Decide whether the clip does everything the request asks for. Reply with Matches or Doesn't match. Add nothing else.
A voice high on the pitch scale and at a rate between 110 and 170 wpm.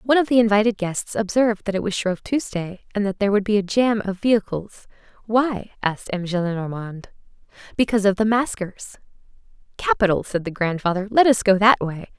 Matches